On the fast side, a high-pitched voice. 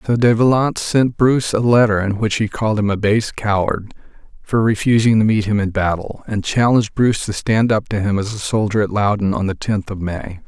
No: fast, 230 wpm; low, 105 Hz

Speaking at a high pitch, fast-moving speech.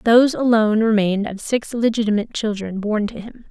No: high, 220 Hz; average, 170 wpm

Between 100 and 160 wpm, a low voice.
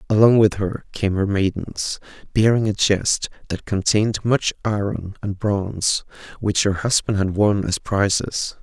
Yes: average, 155 wpm; low, 100 Hz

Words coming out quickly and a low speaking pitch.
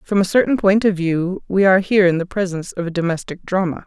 No: fast, 250 wpm; medium, 185 Hz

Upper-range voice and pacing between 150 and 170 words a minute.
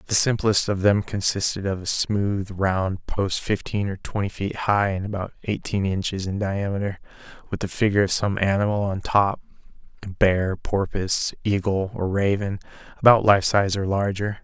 No: low, 100 Hz; average, 160 wpm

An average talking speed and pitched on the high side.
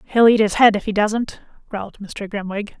No: fast, 215 wpm; high, 210 Hz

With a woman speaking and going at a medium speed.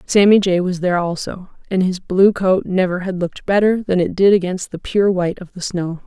No: female; fast, 230 wpm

